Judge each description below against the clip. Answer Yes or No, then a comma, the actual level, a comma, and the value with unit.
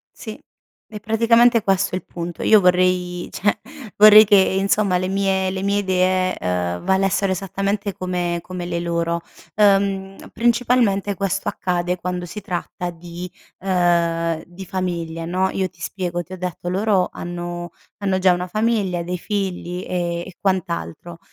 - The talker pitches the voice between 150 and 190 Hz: Yes, medium, 185 Hz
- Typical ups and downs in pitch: No, narrow, 2.1 semitones